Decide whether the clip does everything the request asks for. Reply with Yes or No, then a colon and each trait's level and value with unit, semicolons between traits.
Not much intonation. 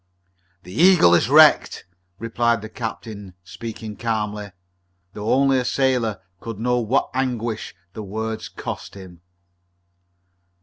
No: average, 3.0 semitones